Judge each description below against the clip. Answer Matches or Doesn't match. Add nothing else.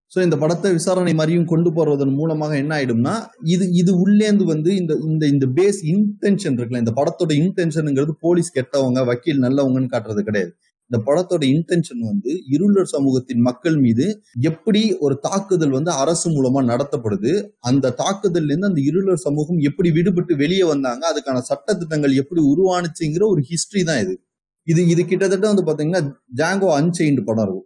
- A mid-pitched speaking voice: Matches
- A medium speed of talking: Doesn't match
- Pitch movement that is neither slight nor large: Matches